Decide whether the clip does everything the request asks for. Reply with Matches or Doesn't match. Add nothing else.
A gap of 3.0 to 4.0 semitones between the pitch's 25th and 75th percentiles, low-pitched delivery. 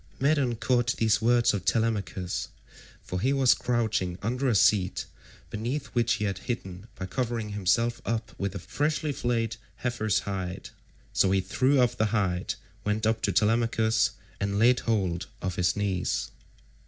Matches